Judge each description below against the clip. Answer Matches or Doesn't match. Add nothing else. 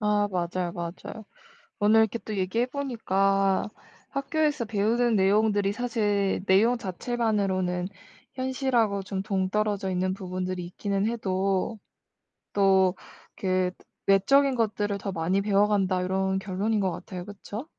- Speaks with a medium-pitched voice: Doesn't match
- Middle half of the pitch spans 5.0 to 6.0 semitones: Doesn't match